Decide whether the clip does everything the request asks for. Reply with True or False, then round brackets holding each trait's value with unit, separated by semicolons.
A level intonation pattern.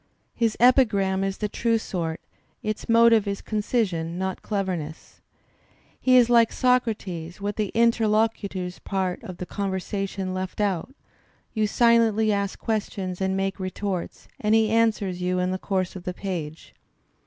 False (3.1 semitones)